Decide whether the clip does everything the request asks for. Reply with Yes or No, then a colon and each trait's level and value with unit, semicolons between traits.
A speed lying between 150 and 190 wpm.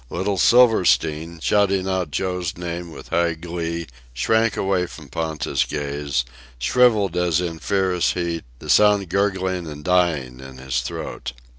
No: average, 140 wpm